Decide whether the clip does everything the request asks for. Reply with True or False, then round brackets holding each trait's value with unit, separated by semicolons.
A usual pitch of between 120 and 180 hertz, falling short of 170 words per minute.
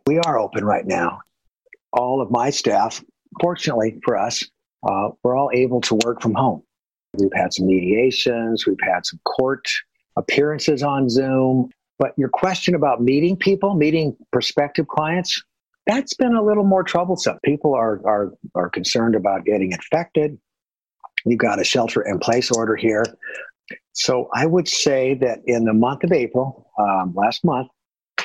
True (135 Hz; 160 wpm)